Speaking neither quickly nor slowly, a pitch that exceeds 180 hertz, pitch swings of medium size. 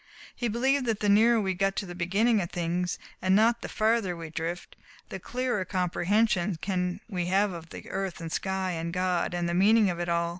No: fast, 210 wpm; high, 190 Hz; average, 3.4 semitones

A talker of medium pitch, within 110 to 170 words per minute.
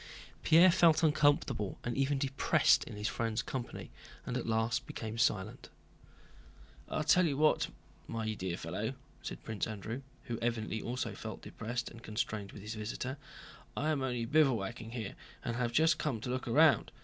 No: low, 120 Hz; average, 165 wpm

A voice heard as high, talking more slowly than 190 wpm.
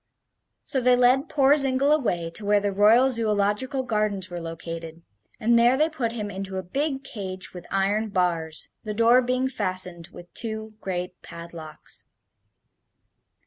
Yes: high, 210 Hz; average, 150 wpm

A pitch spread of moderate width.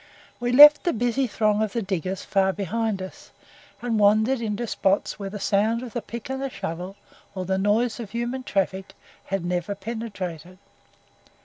Yes: average, 3.6 semitones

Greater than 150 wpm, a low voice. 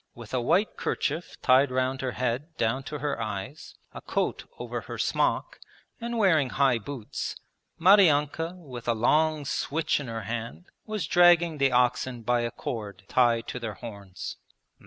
Yes: average, 160 wpm; low, 130 Hz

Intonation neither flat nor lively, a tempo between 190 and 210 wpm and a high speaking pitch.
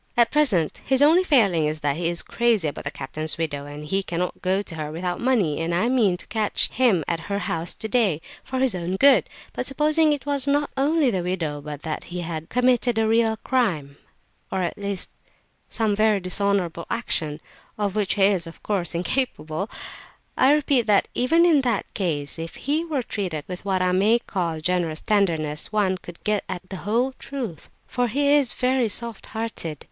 No: wide, 6.6 semitones; average, 195 wpm; high, 200 Hz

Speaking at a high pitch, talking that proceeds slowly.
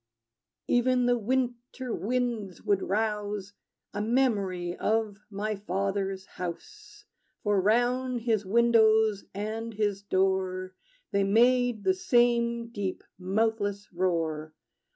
Yes: high, 210 Hz; slow, 105 wpm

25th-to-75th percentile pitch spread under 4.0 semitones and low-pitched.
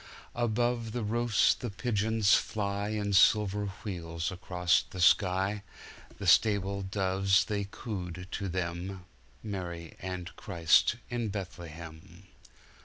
Yes: average, 3.0 semitones; very low, 95 Hz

